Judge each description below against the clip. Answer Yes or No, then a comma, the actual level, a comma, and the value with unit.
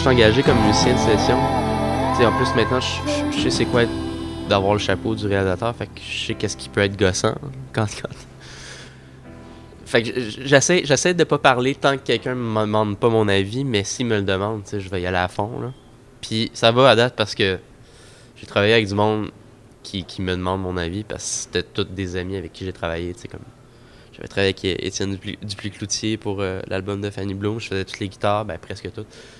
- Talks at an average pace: No, fast, 235 wpm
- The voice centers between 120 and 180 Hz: No, low, 105 Hz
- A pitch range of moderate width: Yes, average, 3.5 semitones